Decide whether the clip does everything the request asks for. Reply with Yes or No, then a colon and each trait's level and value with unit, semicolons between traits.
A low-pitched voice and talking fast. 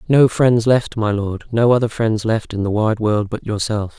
Yes: low, 110 Hz; fast, 225 wpm